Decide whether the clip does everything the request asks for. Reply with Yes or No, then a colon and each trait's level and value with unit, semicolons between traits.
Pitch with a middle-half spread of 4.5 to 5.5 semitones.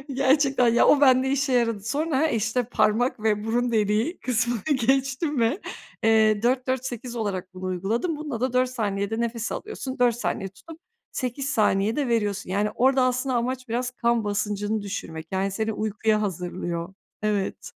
No: average, 3.8 semitones